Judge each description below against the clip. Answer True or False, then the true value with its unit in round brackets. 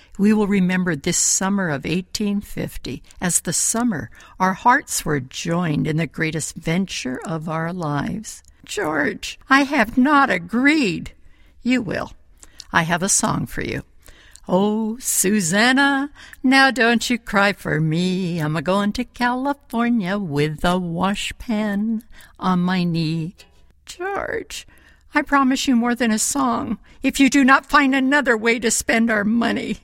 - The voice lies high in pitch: True (210 Hz)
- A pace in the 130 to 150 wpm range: True (145 wpm)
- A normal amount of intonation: False (5.9 semitones)